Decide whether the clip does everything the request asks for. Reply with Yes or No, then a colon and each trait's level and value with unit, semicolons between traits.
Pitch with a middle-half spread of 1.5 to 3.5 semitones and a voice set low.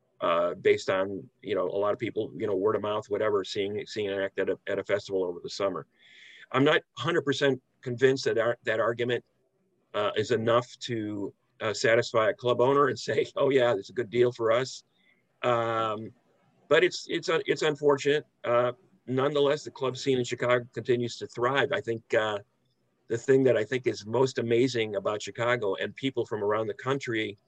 Yes: average, 2.9 semitones; low, 125 Hz